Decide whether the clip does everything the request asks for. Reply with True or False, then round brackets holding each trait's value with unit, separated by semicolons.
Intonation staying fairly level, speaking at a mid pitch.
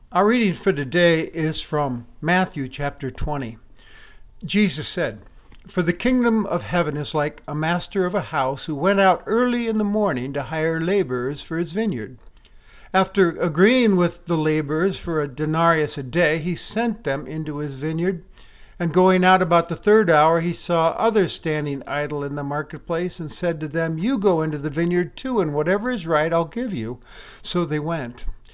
False (4.0 semitones; 170 Hz)